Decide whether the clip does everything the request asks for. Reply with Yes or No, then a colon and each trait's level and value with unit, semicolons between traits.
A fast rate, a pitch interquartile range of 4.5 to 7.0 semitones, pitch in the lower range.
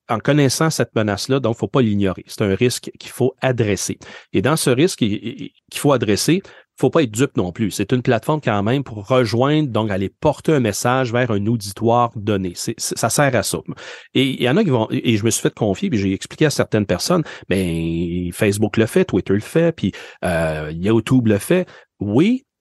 Yes: fast, 225 wpm; average, 4.9 semitones; low, 115 Hz